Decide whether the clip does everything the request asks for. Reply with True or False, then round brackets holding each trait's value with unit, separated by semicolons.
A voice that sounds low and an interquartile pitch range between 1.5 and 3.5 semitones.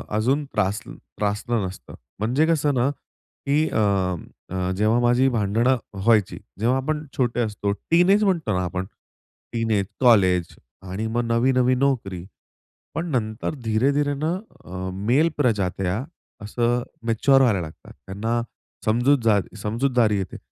False (115 Hz; 4.7 semitones)